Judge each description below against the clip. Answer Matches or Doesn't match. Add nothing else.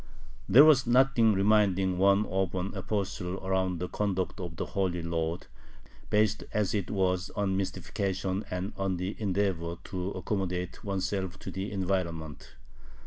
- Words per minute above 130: Matches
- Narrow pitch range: Matches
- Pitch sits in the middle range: Doesn't match